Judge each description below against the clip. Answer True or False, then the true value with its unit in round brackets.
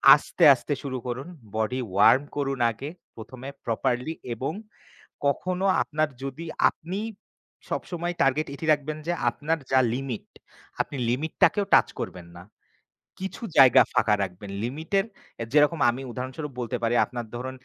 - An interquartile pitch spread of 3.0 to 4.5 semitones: True (4.1 semitones)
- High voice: False (135 Hz)